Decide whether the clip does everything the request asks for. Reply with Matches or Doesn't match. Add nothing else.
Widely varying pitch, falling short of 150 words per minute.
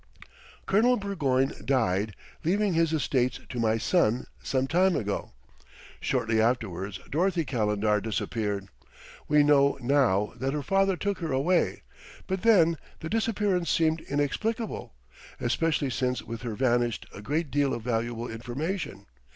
Matches